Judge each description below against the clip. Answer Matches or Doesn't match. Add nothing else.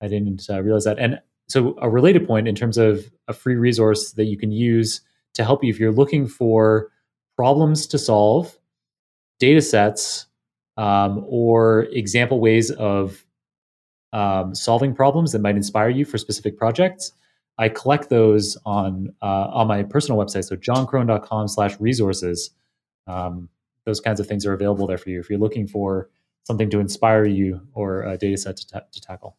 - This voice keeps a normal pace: Matches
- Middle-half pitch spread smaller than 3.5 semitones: Matches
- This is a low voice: Matches